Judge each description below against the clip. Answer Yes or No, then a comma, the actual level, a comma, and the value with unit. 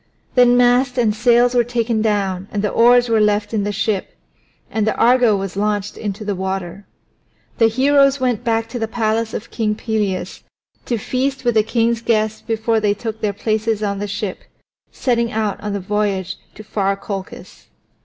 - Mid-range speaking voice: No, high, 220 Hz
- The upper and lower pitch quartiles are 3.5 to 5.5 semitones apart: No, narrow, 2.4 semitones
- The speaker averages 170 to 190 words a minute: Yes, average, 185 wpm